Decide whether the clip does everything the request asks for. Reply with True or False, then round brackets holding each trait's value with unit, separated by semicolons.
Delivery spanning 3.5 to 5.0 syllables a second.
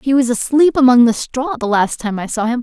False (5.7 syllables/s)